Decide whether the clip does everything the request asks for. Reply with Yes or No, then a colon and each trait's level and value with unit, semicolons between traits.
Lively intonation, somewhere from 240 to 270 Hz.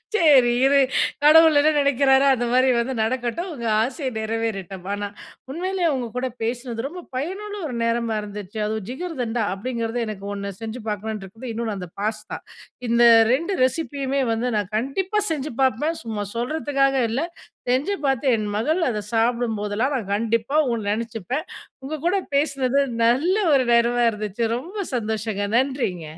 No: average, 4.1 semitones; high, 245 Hz